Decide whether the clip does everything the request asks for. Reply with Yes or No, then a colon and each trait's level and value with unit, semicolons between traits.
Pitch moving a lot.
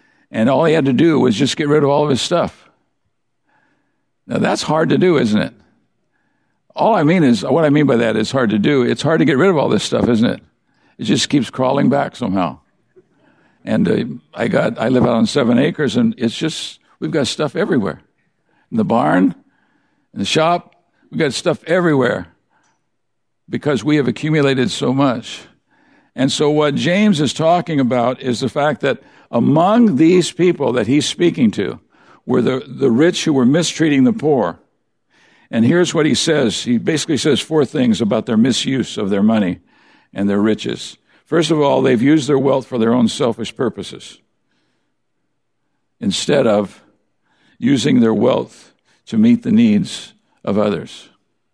Yes: wide, 6.8 semitones